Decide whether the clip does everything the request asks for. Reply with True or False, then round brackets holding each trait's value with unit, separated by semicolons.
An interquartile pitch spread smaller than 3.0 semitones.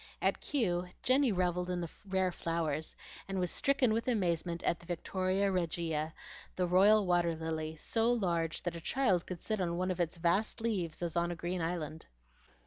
True (2.5 semitones)